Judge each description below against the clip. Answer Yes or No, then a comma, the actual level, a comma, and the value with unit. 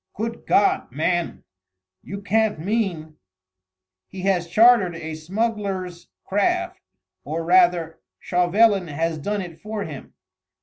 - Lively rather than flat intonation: No, average, 4.2 semitones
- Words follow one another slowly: Yes, slow, 120 wpm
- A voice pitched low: No, medium, 180 Hz